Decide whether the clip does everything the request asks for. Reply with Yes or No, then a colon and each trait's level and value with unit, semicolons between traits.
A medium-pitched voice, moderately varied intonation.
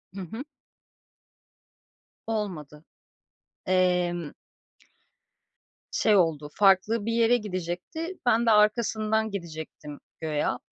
No: high, 195 Hz; average, 4.5 semitones